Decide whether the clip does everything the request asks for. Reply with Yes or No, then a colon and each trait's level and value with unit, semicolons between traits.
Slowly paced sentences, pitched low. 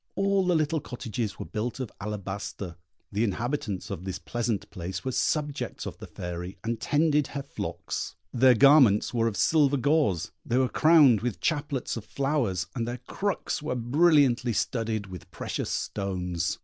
No: average, 160 wpm; low, 120 Hz